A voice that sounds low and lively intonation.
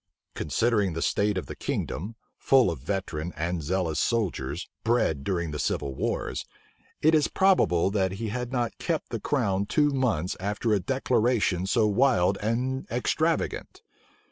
Yes: low, 100 Hz; wide, 5.7 semitones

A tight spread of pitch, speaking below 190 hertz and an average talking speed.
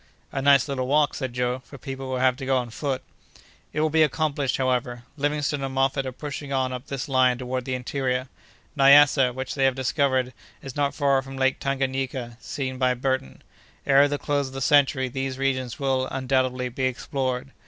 Yes: narrow, 1.3 semitones; low, 135 Hz; average, 195 wpm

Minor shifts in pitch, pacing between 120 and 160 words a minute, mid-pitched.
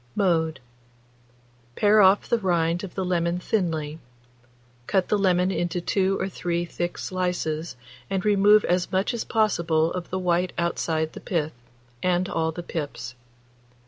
Yes: narrow, 2.3 semitones; average, 145 wpm; medium, 180 Hz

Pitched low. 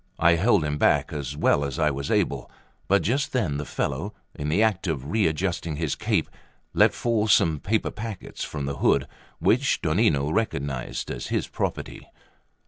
Yes: very low, 80 Hz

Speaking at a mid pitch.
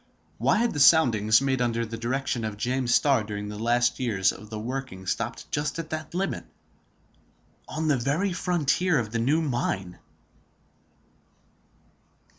No: low, 125 Hz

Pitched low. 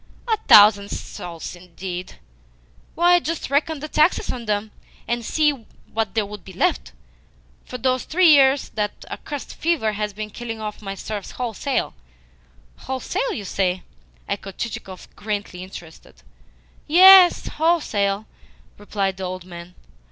No: high, 215 Hz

